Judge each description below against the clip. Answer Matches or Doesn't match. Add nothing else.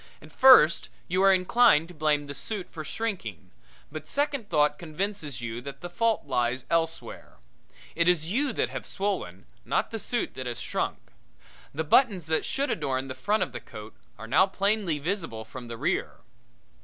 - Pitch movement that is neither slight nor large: Doesn't match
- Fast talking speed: Doesn't match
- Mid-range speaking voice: Matches